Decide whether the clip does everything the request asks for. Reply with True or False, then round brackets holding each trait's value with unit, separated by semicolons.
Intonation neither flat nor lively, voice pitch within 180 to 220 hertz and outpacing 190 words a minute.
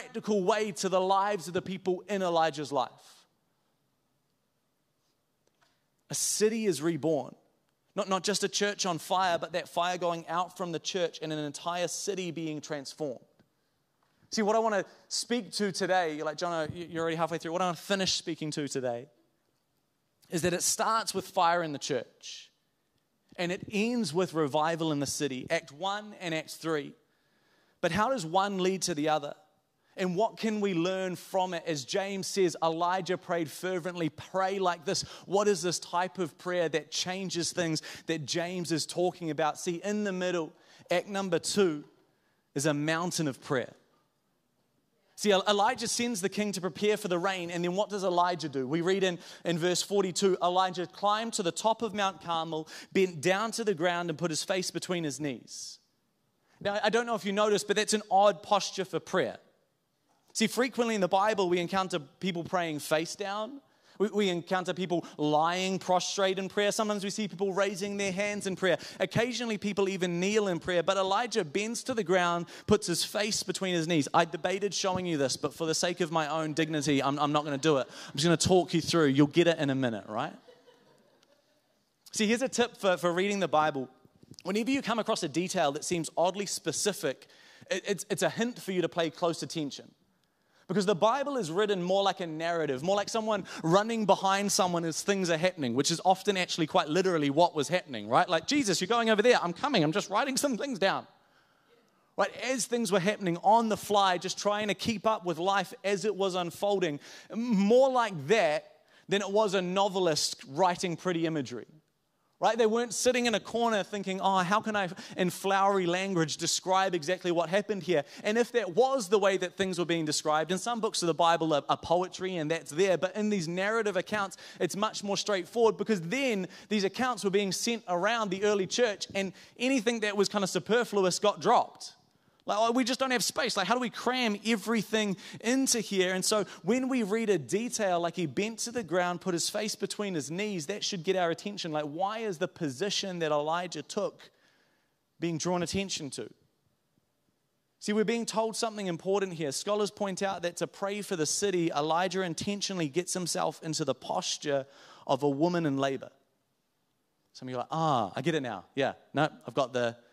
True (3.6 semitones; 185 Hz; 200 wpm)